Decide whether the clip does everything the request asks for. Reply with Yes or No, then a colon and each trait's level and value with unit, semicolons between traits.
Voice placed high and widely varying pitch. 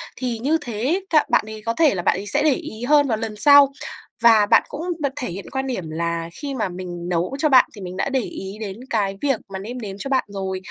Yes: high, 220 Hz; wide, 5.8 semitones